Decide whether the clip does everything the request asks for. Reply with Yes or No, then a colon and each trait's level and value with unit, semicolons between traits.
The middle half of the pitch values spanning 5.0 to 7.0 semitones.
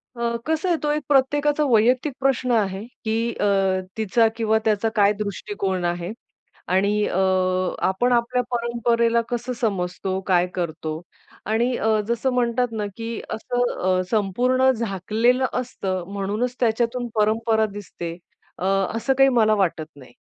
No: average, 3.8 semitones